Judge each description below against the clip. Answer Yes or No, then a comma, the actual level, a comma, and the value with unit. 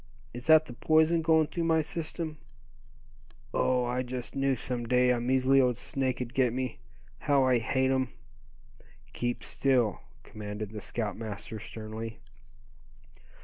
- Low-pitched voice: Yes, low, 125 Hz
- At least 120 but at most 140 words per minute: Yes, slow, 135 wpm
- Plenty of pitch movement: No, narrow, 2.6 semitones